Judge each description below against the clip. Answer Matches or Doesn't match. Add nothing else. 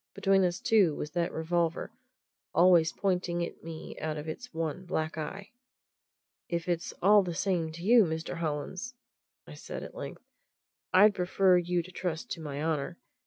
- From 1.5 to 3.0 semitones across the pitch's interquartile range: Matches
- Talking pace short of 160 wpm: Doesn't match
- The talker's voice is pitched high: Doesn't match